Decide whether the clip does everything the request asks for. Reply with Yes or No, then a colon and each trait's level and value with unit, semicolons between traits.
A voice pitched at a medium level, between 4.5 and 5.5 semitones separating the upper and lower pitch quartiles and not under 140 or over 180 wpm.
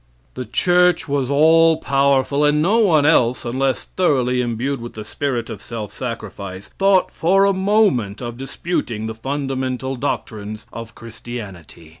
No: low, 130 Hz; average, 5.2 semitones; average, 145 wpm